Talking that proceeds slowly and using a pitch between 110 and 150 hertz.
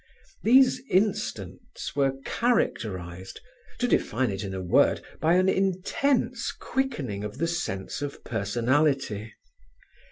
Yes: slow, 100 wpm; medium, 140 Hz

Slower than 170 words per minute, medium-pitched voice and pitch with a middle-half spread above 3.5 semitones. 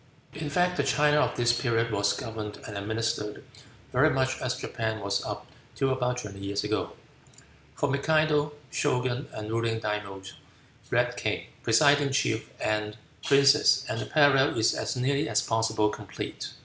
No: average, 155 wpm; low, 120 Hz; average, 4.6 semitones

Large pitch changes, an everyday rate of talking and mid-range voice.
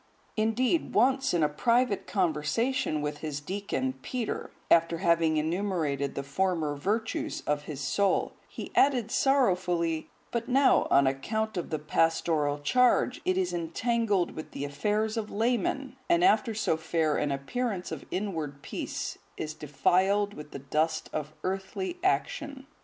Yes: wide, 7.1 semitones; average, 145 wpm; medium, 180 Hz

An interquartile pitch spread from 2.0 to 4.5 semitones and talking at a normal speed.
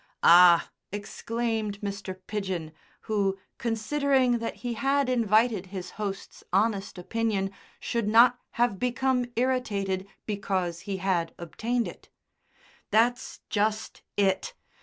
No: average, 3.7 semitones; slow, 110 wpm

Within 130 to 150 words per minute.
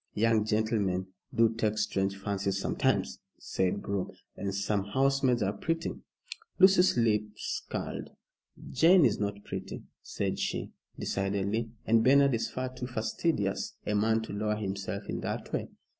Yes: average, 145 wpm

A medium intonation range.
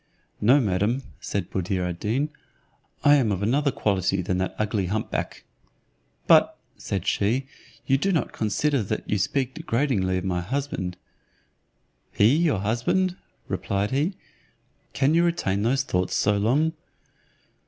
No: wide, 6.4 semitones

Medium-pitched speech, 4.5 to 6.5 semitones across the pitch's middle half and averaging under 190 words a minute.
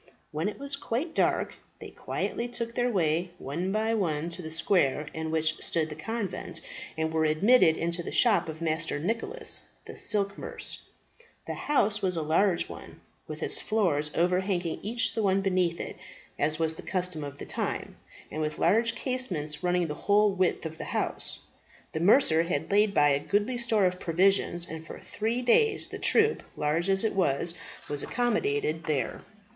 Yes: medium, 180 Hz; average, 5.2 semitones; average, 180 wpm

